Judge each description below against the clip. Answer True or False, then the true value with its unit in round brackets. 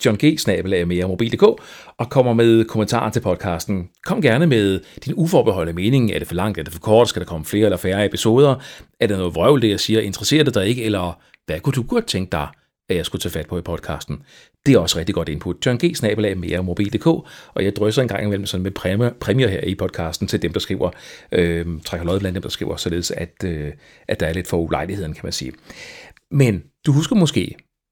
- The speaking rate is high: True (235 wpm)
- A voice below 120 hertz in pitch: True (100 Hz)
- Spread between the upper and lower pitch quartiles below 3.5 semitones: False (5.0 semitones)